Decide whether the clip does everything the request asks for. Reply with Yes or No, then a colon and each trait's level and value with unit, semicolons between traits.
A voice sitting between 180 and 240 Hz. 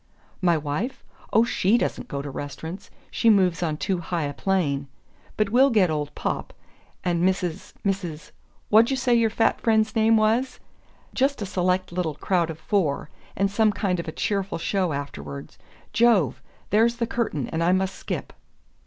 Yes: high, 190 Hz